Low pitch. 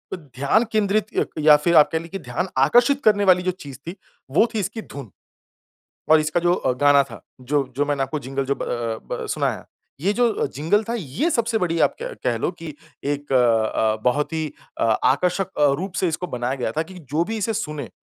No: medium, 155 Hz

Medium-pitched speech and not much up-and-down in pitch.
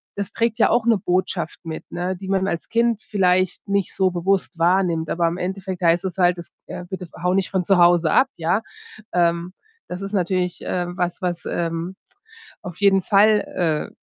Yes: medium, 180 Hz; narrow, 2.1 semitones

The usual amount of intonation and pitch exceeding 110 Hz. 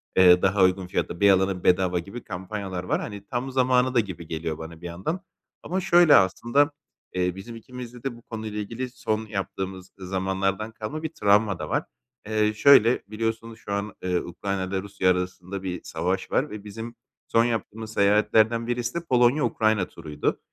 No: average, 4.0 semitones; low, 105 Hz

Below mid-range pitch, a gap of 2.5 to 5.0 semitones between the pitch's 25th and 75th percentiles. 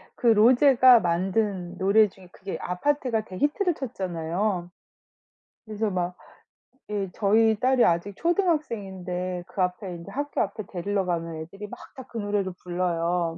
No: high, 195 Hz; average, 4.0 semitones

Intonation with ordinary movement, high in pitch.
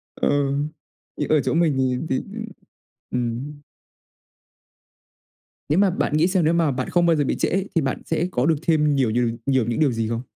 No: average, 4.5 semitones; medium, 145 Hz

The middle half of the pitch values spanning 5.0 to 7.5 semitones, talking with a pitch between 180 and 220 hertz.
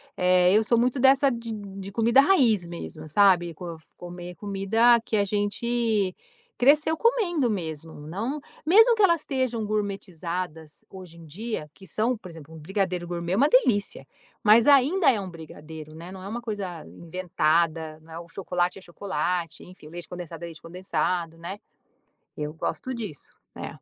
Yes: wide, 5.4 semitones; high, 190 Hz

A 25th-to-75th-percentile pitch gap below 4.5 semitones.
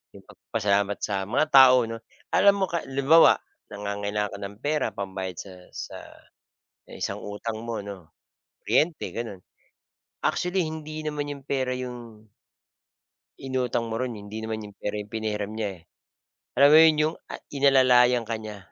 No: average, 5.3 semitones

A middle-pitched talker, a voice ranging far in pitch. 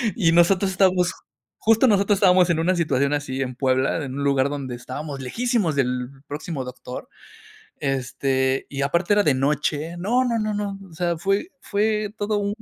Yes: medium, 165 Hz; wide, 6.7 semitones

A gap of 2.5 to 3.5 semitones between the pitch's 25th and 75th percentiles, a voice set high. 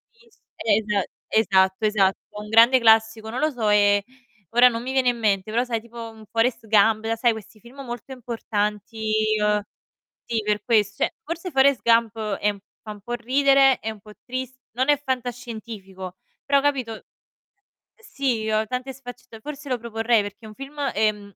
Yes: average, 2.9 semitones; high, 225 Hz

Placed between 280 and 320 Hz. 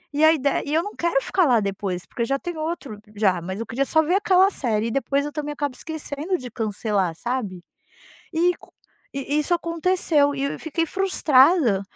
Yes: very high, 285 Hz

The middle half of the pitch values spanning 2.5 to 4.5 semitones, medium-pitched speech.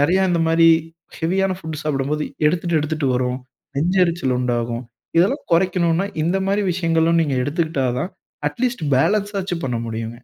No: average, 5.0 semitones; medium, 165 Hz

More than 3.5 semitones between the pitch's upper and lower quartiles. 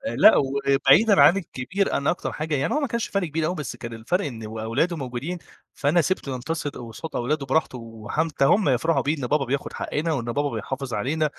Yes: average, 4.5 semitones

